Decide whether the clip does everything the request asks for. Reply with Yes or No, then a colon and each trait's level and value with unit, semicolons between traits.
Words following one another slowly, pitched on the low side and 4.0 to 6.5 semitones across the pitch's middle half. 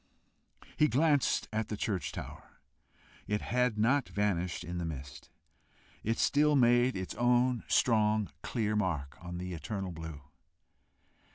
Yes: slow, 125 wpm; low, 105 Hz; wide, 5.5 semitones